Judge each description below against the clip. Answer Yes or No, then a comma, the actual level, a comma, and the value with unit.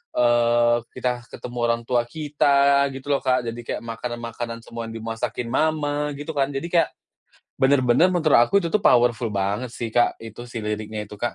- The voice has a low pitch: Yes, low, 120 Hz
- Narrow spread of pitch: No, average, 3.2 semitones